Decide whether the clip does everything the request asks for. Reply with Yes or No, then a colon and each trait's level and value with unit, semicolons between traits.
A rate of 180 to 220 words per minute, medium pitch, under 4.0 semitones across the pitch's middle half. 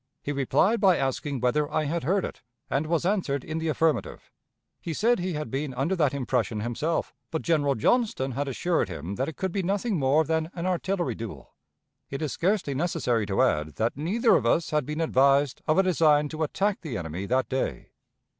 No: average, 200 wpm; medium, 150 Hz; average, 4.6 semitones